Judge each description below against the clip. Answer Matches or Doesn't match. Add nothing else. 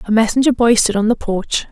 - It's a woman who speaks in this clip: Matches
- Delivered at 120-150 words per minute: Doesn't match